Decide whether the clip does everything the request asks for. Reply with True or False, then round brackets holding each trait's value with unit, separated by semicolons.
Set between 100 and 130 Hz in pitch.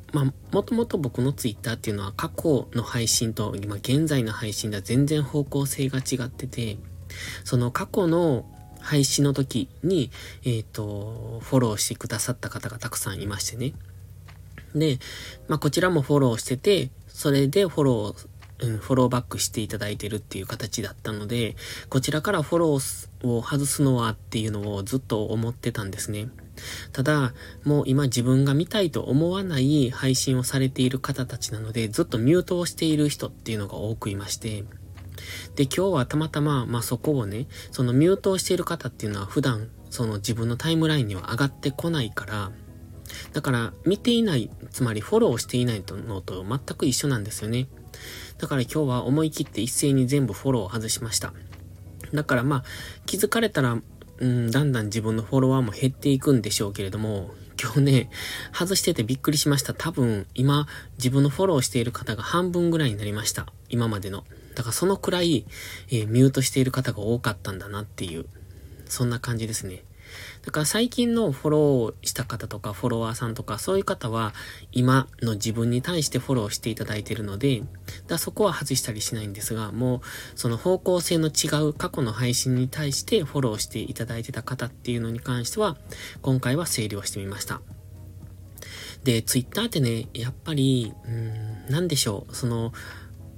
True (120 Hz)